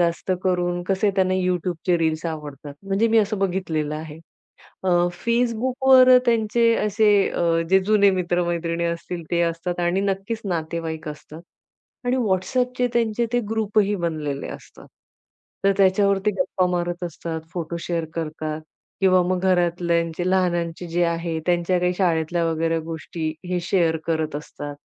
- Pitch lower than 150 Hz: No, medium, 175 Hz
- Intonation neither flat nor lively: Yes, average, 3.0 semitones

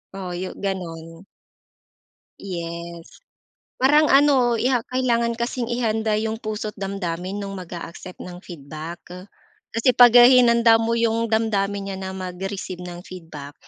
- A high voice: Yes, high, 200 Hz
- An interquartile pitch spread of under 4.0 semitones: No, average, 4.7 semitones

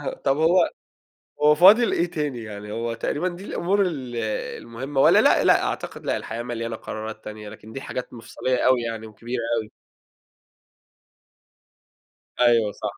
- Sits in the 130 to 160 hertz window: No, low, 120 Hz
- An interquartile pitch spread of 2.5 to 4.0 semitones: No, average, 5.0 semitones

